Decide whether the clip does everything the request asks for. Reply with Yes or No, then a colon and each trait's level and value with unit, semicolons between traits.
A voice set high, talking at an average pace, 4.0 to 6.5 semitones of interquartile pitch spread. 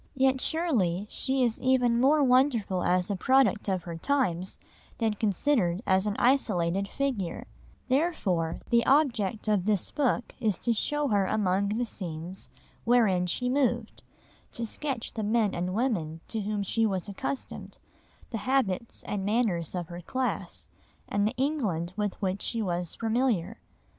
Yes: high, 215 Hz; average, 155 wpm; wide, 5.5 semitones